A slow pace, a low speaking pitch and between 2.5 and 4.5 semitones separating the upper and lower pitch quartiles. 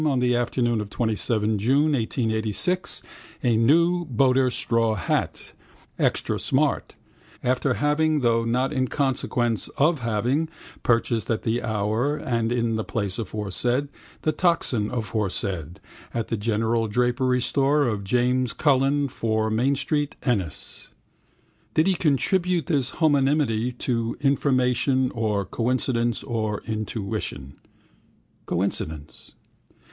Yes: slow, 115 wpm; low, 120 Hz; average, 3.8 semitones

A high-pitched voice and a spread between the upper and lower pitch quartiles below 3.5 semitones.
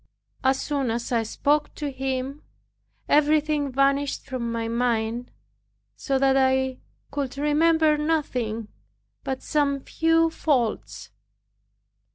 Yes: very high, 270 Hz; average, 3.1 semitones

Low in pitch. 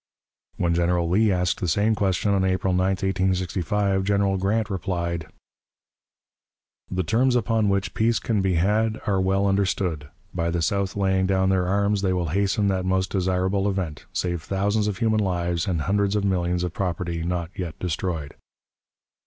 Yes: very low, 95 Hz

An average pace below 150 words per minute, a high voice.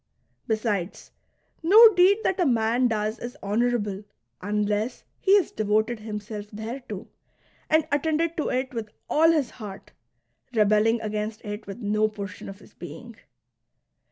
Yes: average, 140 wpm; high, 220 Hz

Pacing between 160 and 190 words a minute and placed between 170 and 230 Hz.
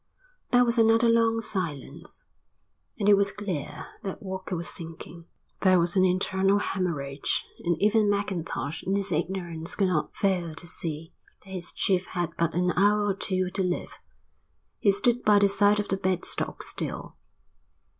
Yes: average, 165 wpm; high, 190 Hz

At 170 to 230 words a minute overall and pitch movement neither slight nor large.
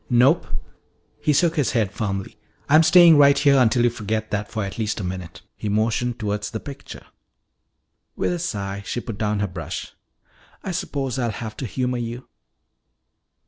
Yes: average, 175 wpm; average, 4.7 semitones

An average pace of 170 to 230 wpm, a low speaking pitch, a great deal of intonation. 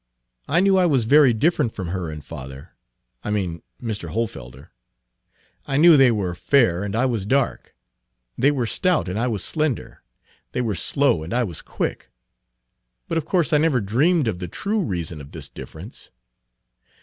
Yes: average, 175 wpm; low, 115 Hz; wide, 8.4 semitones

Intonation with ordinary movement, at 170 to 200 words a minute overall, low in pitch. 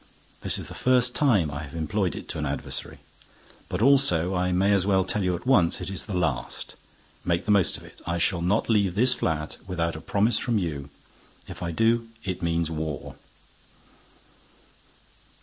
Yes: average, 4.1 semitones; average, 185 wpm; very low, 90 Hz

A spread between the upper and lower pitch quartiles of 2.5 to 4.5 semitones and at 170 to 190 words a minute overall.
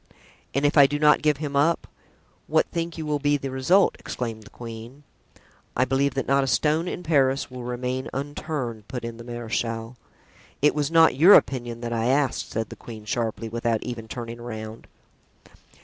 Yes: average, 3.8 semitones; average, 185 wpm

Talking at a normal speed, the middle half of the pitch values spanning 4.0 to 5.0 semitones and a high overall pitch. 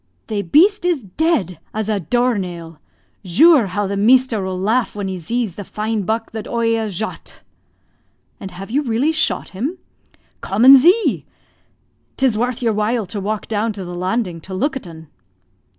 Yes: average, 175 wpm; average, 4.7 semitones; high, 220 Hz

